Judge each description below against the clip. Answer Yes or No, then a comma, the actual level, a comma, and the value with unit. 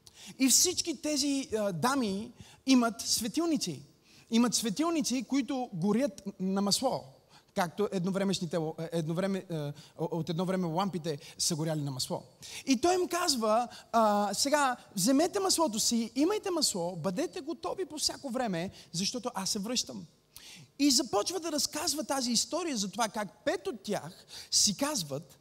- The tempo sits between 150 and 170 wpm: No, average, 140 wpm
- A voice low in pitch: No, high, 225 Hz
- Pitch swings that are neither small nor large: No, wide, 7.5 semitones